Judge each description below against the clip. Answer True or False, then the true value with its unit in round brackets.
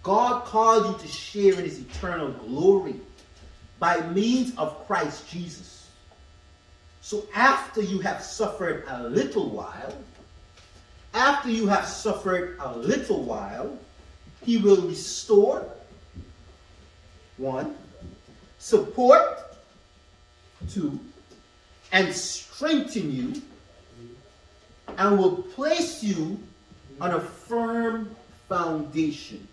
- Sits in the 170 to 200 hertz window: True (185 Hz)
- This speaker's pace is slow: True (95 wpm)